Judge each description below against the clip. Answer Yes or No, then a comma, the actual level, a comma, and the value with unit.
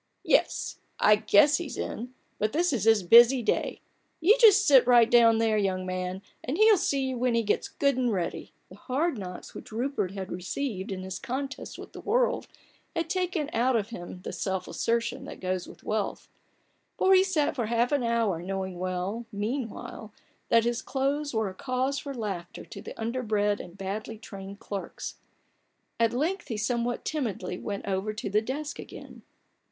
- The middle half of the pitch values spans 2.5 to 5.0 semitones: No, wide, 5.4 semitones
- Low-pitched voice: No, high, 230 Hz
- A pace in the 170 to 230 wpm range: Yes, average, 185 wpm